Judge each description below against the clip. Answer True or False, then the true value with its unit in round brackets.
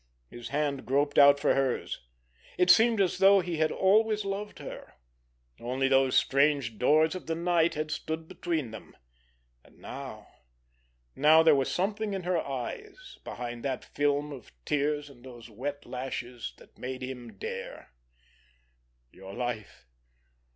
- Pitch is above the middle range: False (140 Hz)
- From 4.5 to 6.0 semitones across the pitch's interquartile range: True (5.4 semitones)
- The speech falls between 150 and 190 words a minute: False (135 wpm)